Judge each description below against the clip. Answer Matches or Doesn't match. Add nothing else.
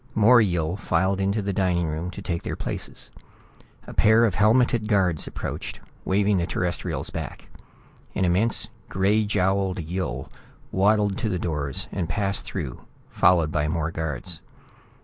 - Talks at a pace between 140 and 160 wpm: Matches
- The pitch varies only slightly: Doesn't match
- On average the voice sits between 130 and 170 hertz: Doesn't match